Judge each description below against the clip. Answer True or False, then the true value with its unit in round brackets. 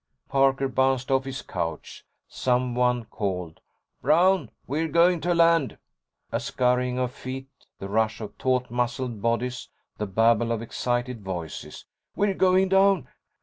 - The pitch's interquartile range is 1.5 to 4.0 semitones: True (3.1 semitones)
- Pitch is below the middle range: True (125 Hz)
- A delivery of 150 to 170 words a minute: False (135 wpm)